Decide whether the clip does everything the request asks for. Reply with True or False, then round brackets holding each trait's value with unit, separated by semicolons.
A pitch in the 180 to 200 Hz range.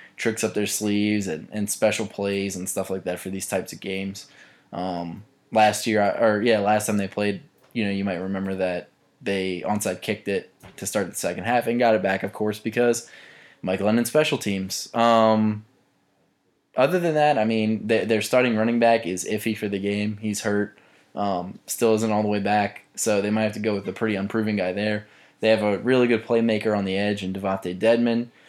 False (105 Hz)